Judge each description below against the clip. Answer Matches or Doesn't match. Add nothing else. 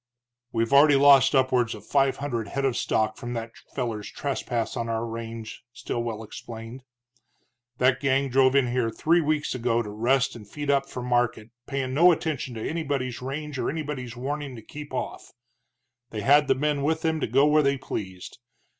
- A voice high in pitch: Doesn't match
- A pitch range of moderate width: Matches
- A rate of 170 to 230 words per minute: Matches